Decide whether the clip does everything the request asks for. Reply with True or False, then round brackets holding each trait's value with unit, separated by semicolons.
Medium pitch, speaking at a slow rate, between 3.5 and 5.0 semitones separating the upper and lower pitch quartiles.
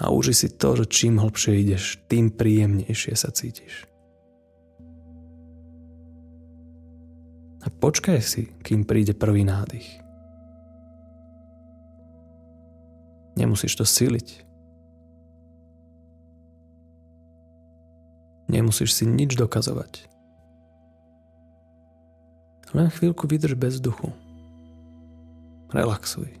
False (80 Hz; 75 wpm; 4.5 semitones)